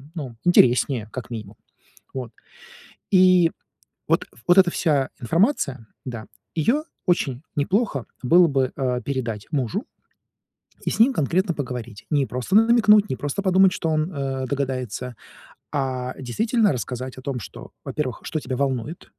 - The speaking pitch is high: No, medium, 140 Hz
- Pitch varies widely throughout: Yes, wide, 5.9 semitones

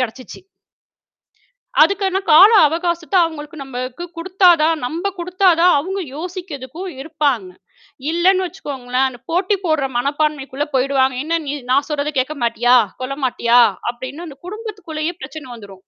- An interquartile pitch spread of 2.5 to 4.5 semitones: No, average, 5.0 semitones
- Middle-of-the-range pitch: No, very high, 305 Hz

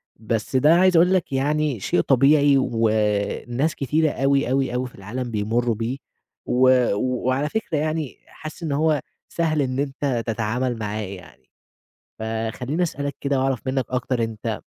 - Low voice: Yes, low, 130 Hz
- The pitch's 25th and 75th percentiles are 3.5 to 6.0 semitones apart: Yes, average, 4.3 semitones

